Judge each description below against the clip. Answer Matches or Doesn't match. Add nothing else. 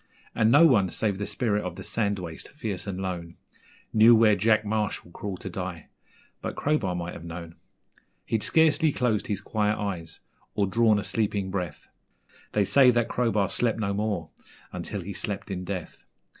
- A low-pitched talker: Matches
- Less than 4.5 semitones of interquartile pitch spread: Matches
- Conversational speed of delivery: Matches